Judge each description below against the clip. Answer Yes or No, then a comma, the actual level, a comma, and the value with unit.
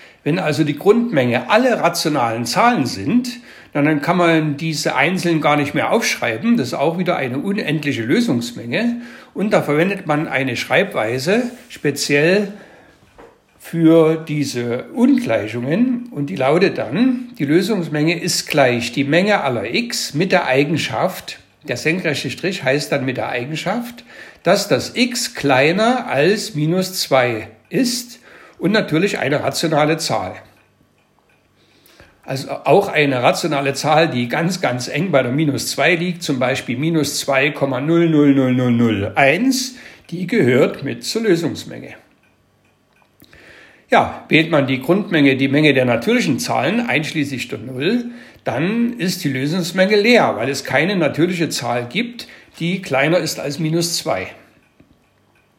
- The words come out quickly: No, average, 135 wpm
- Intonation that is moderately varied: No, wide, 5.9 semitones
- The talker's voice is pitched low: No, medium, 155 Hz